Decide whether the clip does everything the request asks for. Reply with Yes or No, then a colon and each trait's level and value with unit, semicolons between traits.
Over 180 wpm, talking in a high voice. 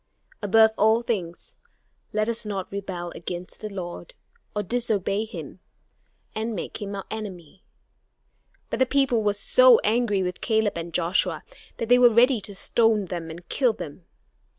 No: average, 155 wpm; high, 210 Hz